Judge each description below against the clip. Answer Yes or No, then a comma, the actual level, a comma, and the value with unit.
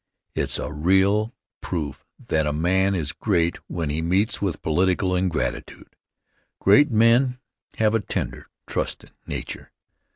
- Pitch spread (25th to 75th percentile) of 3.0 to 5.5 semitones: Yes, average, 4.6 semitones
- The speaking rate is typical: No, slow, 130 wpm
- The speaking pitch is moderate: No, very low, 95 Hz